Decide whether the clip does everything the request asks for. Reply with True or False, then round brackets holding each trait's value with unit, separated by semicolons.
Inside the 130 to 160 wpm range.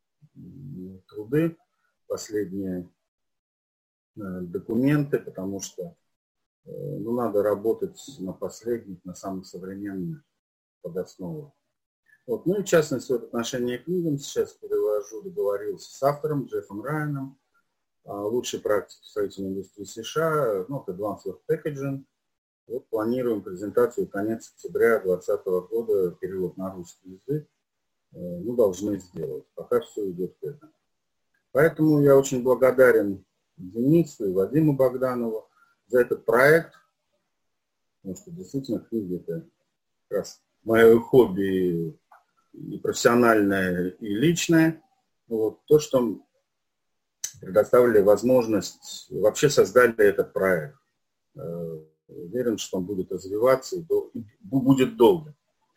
False (110 wpm)